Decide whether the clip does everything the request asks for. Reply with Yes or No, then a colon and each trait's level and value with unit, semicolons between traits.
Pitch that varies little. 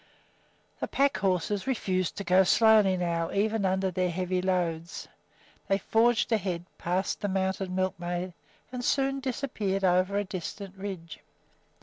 Yes: narrow, 2.1 semitones